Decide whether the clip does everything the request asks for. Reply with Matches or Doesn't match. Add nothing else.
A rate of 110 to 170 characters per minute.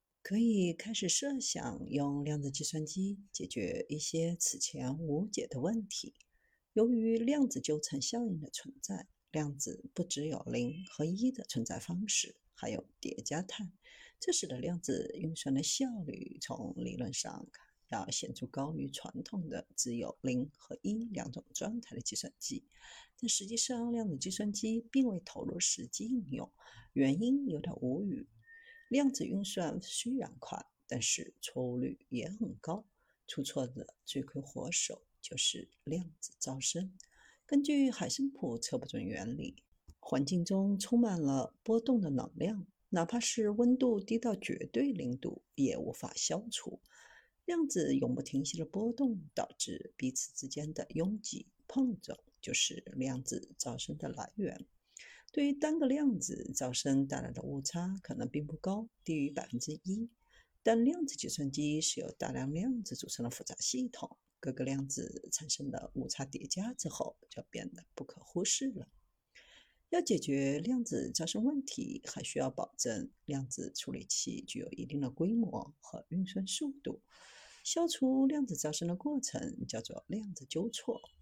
Doesn't match